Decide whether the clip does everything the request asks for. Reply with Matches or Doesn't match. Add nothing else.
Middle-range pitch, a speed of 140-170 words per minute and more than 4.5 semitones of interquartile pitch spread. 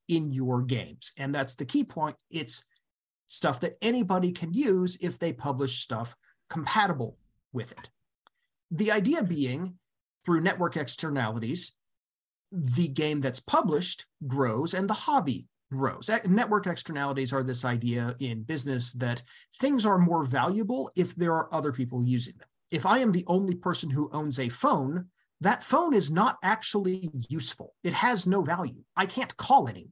Matches